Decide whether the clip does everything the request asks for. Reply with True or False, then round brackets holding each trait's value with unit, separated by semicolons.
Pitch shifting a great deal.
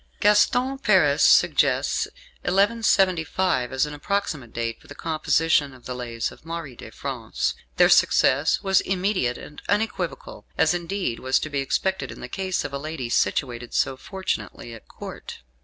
True (6.7 semitones)